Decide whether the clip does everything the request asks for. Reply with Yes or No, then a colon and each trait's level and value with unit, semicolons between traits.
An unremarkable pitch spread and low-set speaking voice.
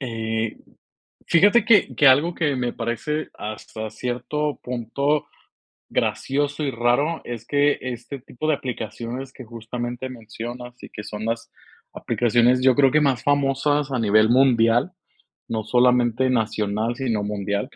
Yes: average, 3.4 semitones; low, 125 Hz